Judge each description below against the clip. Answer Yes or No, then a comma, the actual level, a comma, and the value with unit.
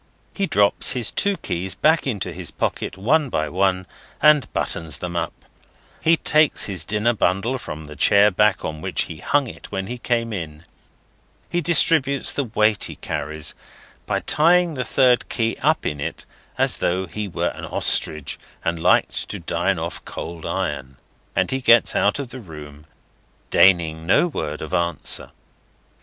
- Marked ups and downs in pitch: Yes, wide, 8.1 semitones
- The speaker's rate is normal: Yes, average, 170 wpm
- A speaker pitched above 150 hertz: No, low, 100 Hz